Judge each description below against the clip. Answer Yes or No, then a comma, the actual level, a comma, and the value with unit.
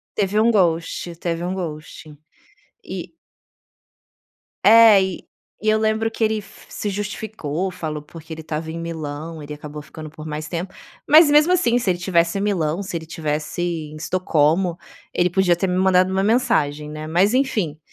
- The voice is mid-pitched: Yes, medium, 175 Hz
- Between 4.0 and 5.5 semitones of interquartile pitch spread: Yes, average, 4.6 semitones